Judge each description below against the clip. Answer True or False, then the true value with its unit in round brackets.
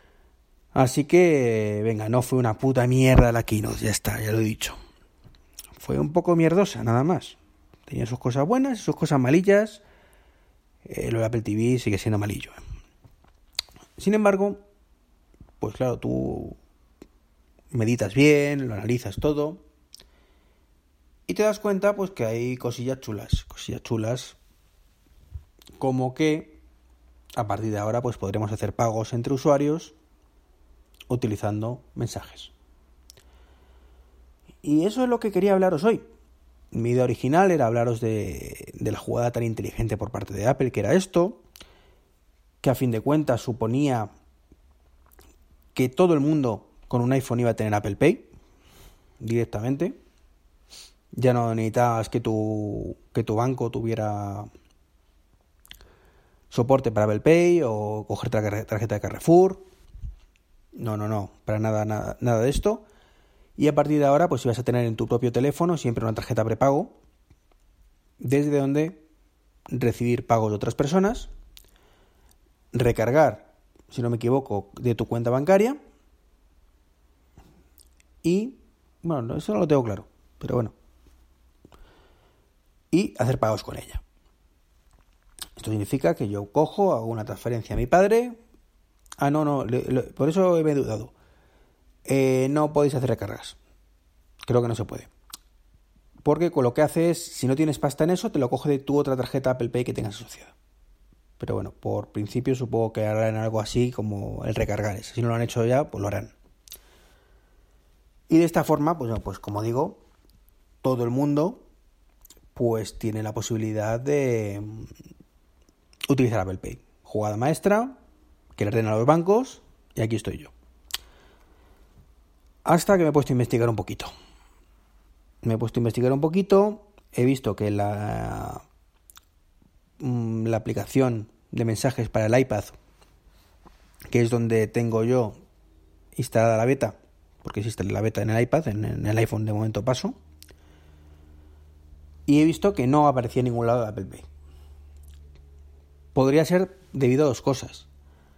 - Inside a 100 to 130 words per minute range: False (150 wpm)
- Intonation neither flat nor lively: False (8.4 semitones)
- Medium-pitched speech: False (110 Hz)